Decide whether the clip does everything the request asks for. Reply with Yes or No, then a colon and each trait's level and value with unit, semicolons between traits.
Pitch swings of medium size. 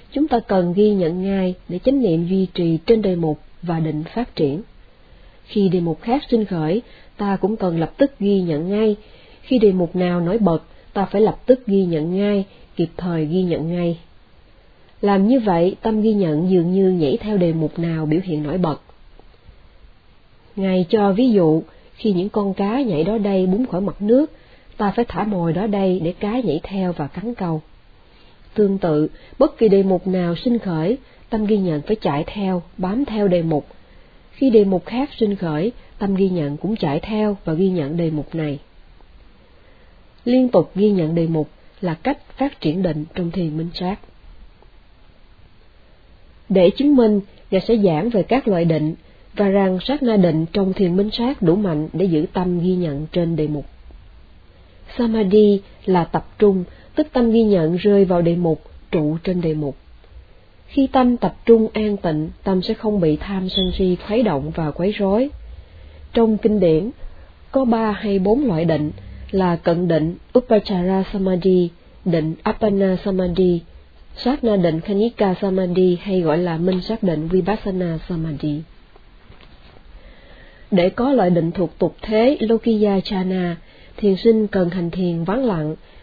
Yes: average, 4.3 semitones